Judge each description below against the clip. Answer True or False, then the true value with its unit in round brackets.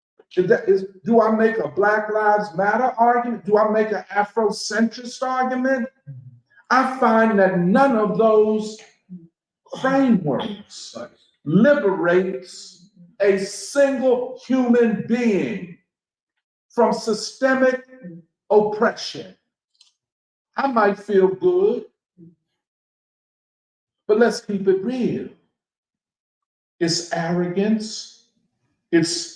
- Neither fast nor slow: False (90 wpm)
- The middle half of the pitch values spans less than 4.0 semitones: False (4.3 semitones)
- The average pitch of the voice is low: False (215 Hz)